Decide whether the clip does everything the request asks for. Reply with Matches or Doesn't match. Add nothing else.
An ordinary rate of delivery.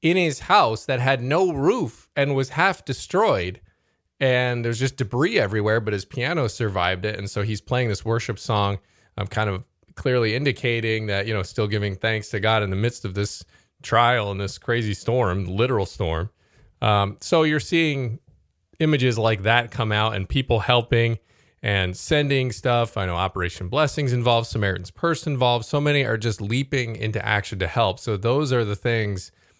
Matches